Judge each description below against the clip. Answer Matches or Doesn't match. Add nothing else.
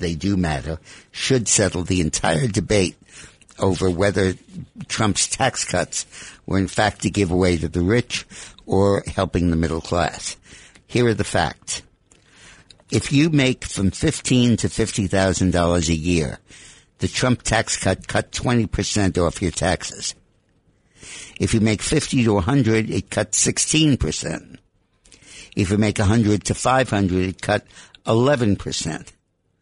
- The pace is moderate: Matches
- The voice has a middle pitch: Doesn't match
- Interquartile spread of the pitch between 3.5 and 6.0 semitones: Matches